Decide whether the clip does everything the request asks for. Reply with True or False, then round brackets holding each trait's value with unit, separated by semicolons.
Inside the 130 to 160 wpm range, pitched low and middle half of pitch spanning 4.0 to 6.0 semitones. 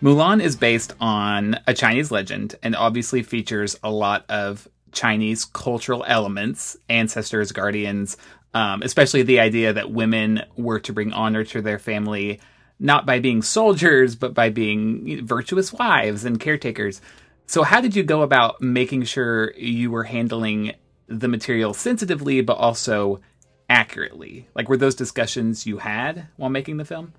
False (150 wpm; 115 Hz; 3.3 semitones)